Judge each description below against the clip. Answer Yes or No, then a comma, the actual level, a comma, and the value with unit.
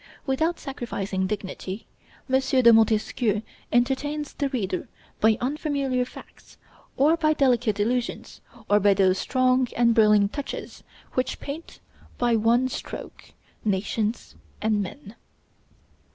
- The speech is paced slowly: Yes, slow, 115 wpm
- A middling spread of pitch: Yes, average, 4.1 semitones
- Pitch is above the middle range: Yes, high, 240 Hz